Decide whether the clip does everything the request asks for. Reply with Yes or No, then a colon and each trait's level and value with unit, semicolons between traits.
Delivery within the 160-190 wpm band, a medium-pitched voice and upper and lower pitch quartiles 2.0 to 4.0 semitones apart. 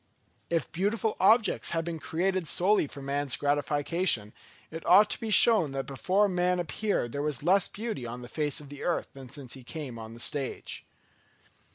No: average, 185 wpm; medium, 160 Hz; wide, 5.4 semitones